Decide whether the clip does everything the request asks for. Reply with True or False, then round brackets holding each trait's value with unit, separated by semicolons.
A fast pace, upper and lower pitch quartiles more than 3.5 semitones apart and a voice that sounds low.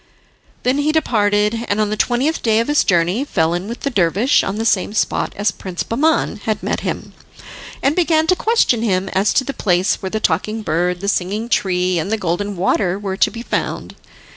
False (210 wpm; 4.4 semitones; 210 Hz)